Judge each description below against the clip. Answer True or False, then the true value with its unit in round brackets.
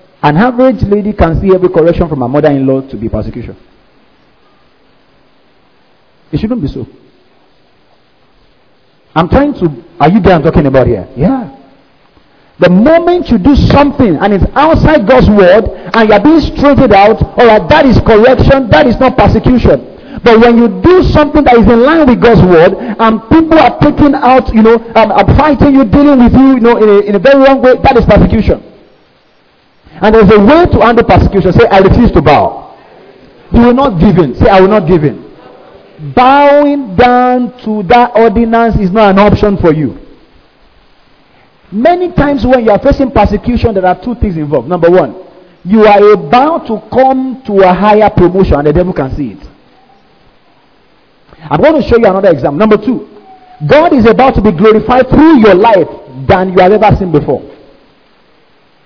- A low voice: False (215 Hz)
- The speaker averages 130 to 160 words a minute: False (180 wpm)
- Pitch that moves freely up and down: True (5.9 semitones)